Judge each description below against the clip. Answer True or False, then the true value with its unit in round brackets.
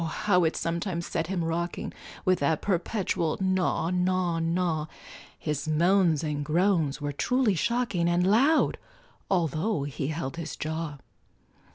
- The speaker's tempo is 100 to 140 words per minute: True (135 wpm)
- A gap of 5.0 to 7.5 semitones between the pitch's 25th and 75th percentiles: False (2.9 semitones)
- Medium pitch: True (170 Hz)